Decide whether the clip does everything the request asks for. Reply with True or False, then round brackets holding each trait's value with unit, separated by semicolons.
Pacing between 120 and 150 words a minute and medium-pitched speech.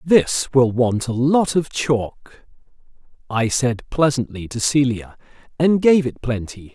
False (140 wpm; 130 Hz)